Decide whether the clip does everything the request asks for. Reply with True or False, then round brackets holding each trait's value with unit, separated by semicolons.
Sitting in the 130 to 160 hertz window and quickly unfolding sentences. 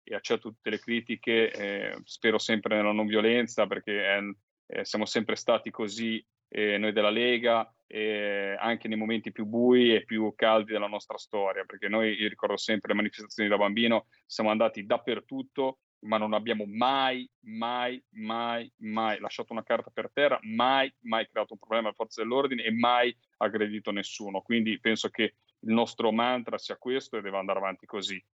False (110 Hz; 175 wpm)